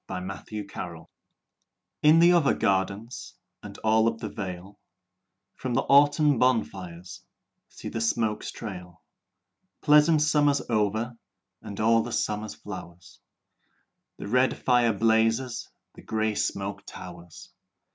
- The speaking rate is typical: No, slow, 120 wpm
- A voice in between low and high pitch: No, low, 110 Hz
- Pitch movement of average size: Yes, average, 4.2 semitones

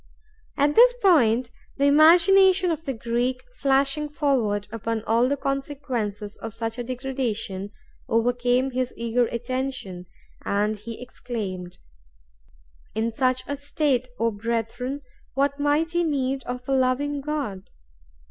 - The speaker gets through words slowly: Yes, slow, 125 wpm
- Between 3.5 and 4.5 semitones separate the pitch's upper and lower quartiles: Yes, average, 3.8 semitones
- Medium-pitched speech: No, very high, 255 Hz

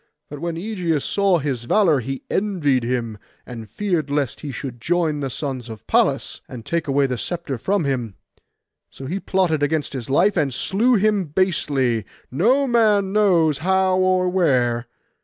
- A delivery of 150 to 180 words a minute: Yes, average, 165 wpm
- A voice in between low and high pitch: Yes, medium, 155 Hz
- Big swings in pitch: Yes, wide, 6.3 semitones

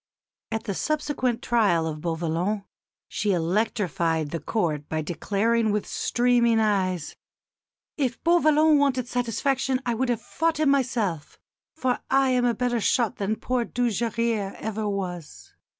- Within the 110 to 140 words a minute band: Yes, slow, 135 wpm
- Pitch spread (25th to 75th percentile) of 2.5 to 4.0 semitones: No, average, 5.1 semitones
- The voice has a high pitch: Yes, high, 225 Hz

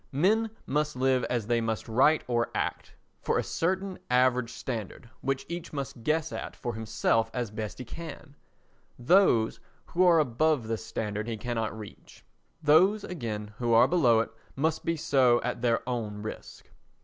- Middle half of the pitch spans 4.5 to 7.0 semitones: Yes, wide, 5.4 semitones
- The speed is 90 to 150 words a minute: No, average, 160 wpm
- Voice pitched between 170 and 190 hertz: No, low, 125 Hz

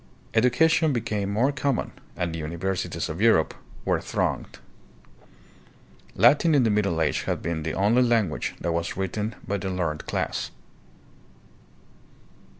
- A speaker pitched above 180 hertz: No, low, 100 Hz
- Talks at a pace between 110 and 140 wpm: Yes, slow, 135 wpm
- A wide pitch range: Yes, wide, 5.8 semitones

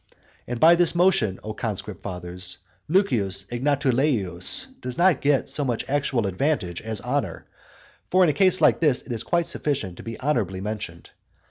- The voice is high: No, low, 125 Hz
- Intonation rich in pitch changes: Yes, wide, 7.4 semitones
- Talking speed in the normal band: Yes, average, 165 wpm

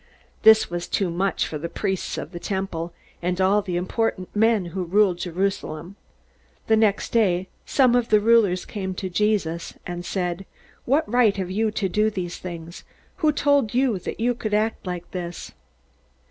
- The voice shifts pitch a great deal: No, average, 3.6 semitones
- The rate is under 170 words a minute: No, average, 175 wpm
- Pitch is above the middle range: Yes, high, 195 Hz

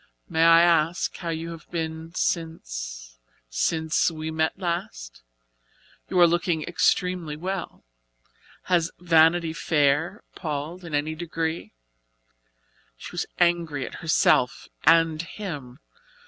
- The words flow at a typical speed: No, slow, 115 wpm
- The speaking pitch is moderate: Yes, medium, 160 Hz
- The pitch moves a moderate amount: No, narrow, 2.1 semitones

